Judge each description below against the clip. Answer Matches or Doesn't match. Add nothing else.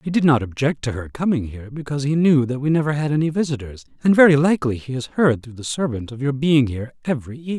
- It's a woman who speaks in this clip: Doesn't match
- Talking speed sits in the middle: Doesn't match